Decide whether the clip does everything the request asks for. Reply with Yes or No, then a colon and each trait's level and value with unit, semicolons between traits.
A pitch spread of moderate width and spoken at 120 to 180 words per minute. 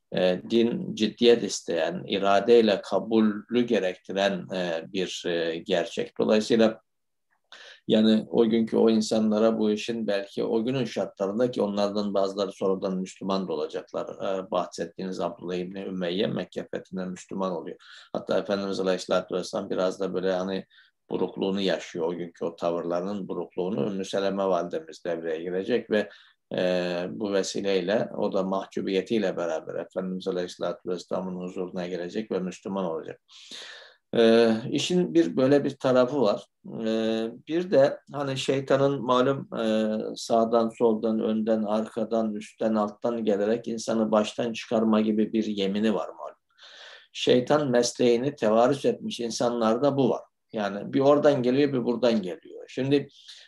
Yes: average, 3.7 semitones; average, 125 wpm